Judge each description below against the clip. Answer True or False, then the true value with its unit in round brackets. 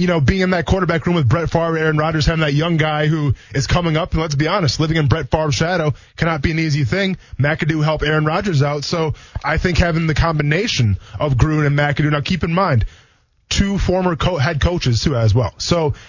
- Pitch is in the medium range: True (155 Hz)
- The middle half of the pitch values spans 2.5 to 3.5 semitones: True (2.9 semitones)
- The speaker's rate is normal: False (230 wpm)